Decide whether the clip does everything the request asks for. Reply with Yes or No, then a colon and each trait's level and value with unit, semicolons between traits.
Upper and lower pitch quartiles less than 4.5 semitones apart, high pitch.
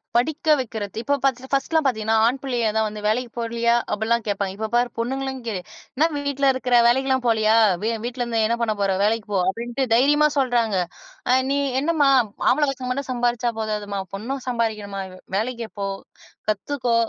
Yes: average, 3.3 semitones; high, 240 Hz